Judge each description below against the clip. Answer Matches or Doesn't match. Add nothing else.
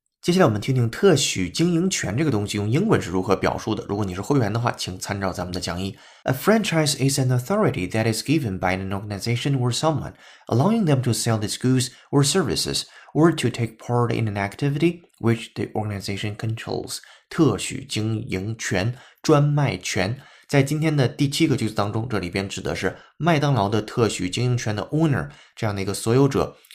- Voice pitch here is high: Doesn't match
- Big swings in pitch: Matches